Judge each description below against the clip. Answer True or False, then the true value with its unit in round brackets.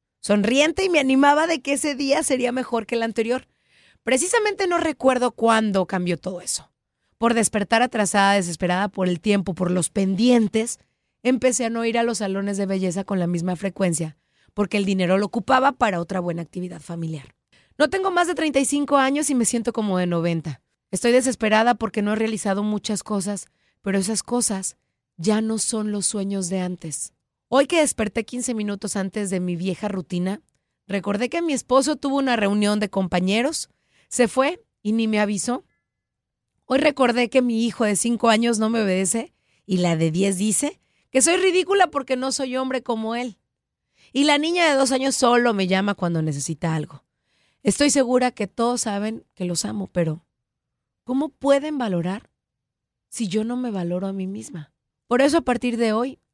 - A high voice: True (220 Hz)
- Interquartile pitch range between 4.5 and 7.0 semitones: True (5.2 semitones)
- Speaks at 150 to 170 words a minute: False (180 wpm)